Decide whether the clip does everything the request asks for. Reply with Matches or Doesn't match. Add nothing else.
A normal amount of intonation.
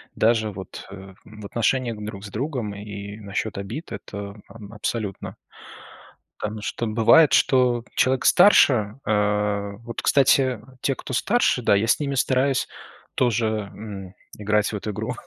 Matches